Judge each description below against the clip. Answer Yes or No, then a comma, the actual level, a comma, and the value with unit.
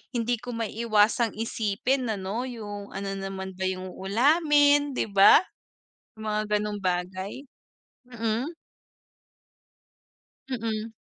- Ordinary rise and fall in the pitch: Yes, average, 3.6 semitones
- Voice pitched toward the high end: Yes, high, 220 Hz